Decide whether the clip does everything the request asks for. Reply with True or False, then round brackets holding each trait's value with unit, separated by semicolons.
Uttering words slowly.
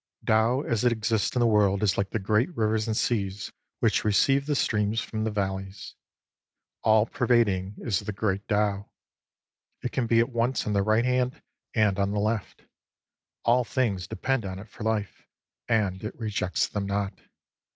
False (175 wpm)